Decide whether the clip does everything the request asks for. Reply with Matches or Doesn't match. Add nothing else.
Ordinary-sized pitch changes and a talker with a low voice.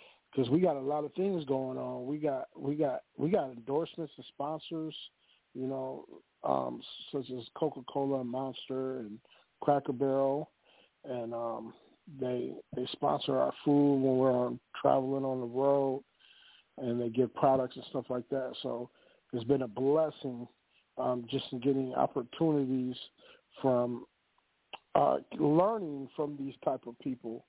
Doesn't match